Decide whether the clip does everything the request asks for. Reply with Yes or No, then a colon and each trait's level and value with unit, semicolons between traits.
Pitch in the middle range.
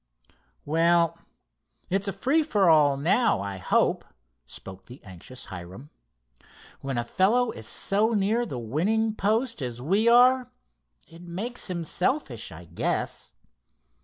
Yes: medium, 175 Hz